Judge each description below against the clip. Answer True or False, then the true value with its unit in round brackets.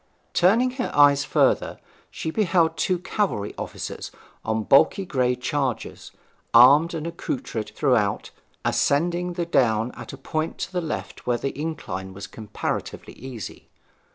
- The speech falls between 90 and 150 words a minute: True (135 wpm)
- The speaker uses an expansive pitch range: True (5.8 semitones)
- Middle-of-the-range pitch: True (145 Hz)